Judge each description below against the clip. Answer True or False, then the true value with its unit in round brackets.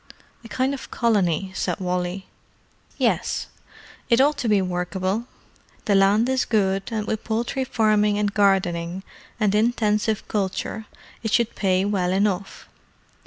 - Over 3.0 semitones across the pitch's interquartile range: False (2.7 semitones)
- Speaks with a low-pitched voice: False (205 Hz)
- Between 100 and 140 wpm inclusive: True (135 wpm)